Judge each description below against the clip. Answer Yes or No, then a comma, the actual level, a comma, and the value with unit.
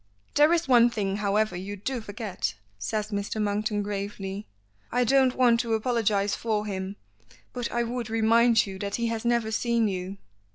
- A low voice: No, high, 220 Hz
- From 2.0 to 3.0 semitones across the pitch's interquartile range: Yes, average, 2.7 semitones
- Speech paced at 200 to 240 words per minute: No, average, 170 wpm